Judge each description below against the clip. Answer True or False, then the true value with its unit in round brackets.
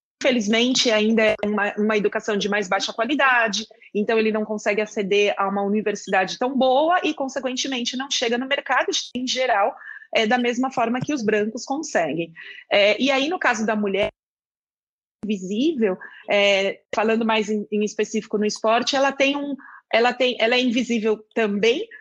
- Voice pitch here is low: False (225 Hz)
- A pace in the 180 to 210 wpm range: False (165 wpm)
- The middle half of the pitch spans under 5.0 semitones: True (3.8 semitones)